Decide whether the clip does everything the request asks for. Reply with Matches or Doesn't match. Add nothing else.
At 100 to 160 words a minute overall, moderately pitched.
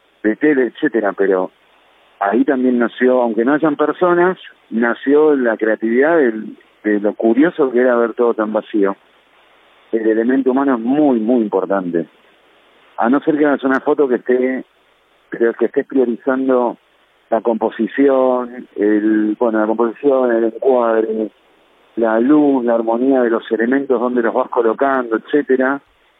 Doesn't match